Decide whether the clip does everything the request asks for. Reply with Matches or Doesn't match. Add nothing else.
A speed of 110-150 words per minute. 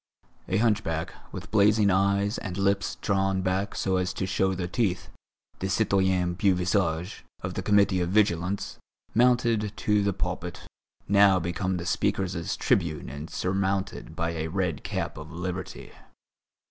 Matches